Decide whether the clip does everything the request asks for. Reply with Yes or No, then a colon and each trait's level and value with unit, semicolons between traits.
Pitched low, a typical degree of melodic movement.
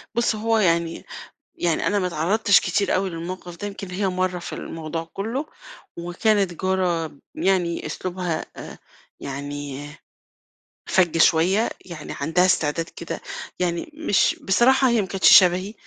No: medium, 180 Hz; average, 3.0 semitones